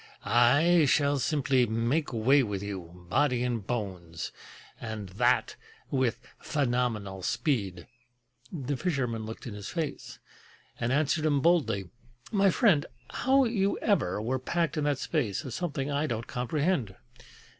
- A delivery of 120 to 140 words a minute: Yes, slow, 135 wpm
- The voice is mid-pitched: No, low, 130 Hz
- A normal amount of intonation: No, wide, 5.7 semitones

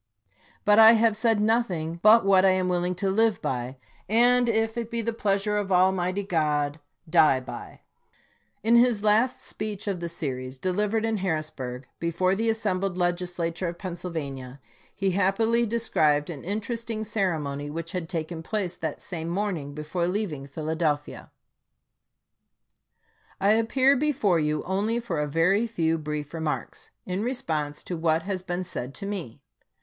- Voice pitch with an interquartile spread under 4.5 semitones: No, average, 5.2 semitones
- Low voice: No, medium, 185 Hz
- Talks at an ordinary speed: Yes, average, 160 wpm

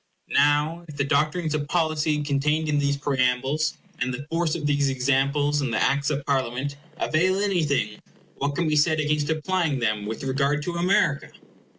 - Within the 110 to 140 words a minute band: No, average, 175 wpm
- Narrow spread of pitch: Yes, narrow, 2.1 semitones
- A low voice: No, medium, 145 Hz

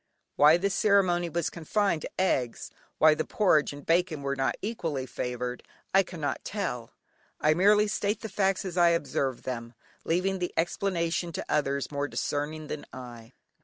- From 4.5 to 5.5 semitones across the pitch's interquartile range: Yes, average, 5.1 semitones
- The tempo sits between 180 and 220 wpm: No, average, 165 wpm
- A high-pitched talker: No, medium, 165 Hz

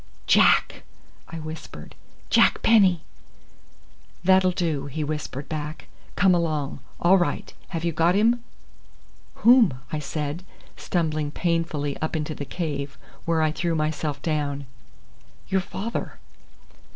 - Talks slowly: Yes, slow, 120 wpm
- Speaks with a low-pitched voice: No, medium, 160 Hz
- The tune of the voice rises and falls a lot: No, average, 3.0 semitones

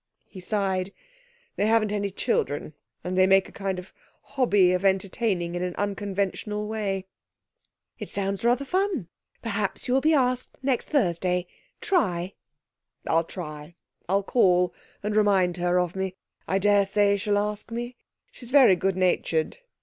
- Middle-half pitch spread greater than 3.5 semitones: No, average, 2.9 semitones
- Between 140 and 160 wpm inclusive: Yes, average, 150 wpm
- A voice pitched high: Yes, high, 195 Hz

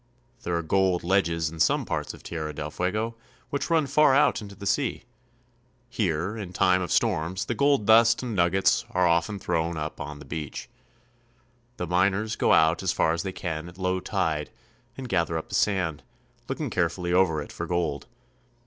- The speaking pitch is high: No, very low, 90 Hz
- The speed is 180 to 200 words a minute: Yes, average, 185 wpm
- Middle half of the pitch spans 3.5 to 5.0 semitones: Yes, average, 3.9 semitones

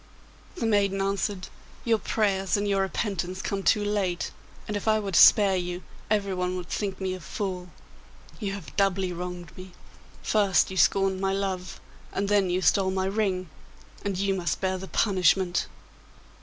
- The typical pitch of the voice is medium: No, high, 195 Hz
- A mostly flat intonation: Yes, narrow, 1.6 semitones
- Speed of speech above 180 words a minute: No, average, 170 wpm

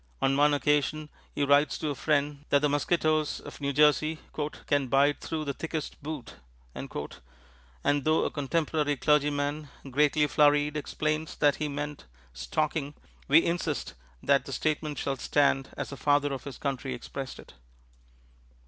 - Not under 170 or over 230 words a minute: No, average, 150 wpm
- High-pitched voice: No, medium, 145 Hz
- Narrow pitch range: Yes, narrow, 1.6 semitones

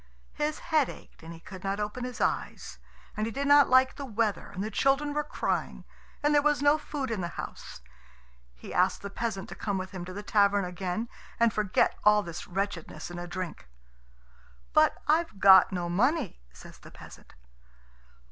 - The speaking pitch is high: Yes, high, 210 Hz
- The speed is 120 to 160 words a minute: No, average, 190 wpm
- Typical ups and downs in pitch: No, wide, 6.6 semitones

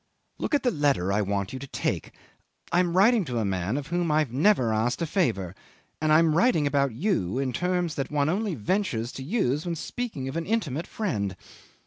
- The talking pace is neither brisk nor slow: No, fast, 210 wpm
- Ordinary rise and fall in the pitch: No, wide, 6.7 semitones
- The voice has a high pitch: No, medium, 150 Hz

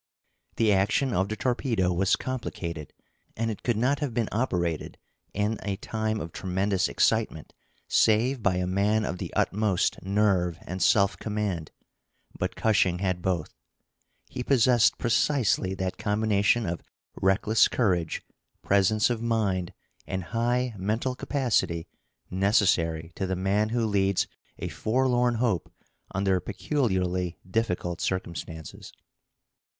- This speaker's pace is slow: Yes, slow, 125 wpm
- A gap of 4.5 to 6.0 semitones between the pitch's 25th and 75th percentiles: No, average, 3.7 semitones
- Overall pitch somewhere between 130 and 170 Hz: No, low, 100 Hz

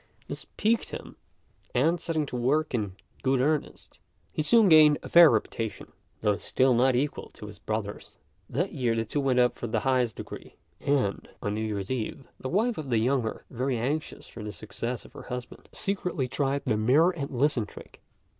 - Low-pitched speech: Yes, low, 130 Hz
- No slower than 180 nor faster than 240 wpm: Yes, average, 190 wpm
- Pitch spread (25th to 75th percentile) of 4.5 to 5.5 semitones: Yes, average, 4.8 semitones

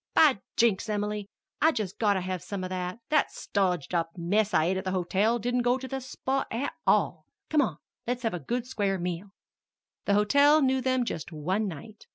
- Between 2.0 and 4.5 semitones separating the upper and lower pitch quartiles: No, average, 5.2 semitones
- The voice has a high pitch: Yes, high, 210 Hz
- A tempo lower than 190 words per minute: No, fast, 205 wpm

